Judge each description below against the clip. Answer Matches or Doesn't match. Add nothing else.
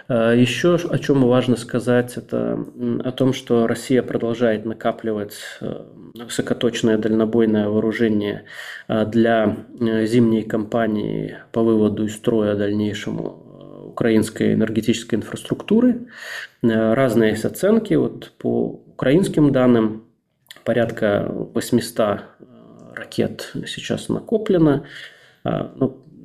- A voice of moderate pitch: Doesn't match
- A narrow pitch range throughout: Matches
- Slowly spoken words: Matches